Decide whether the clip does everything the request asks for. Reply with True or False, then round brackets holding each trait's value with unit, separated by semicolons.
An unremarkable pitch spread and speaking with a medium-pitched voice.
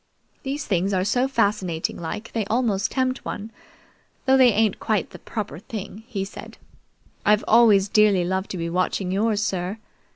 False (3.1 semitones; 210 Hz)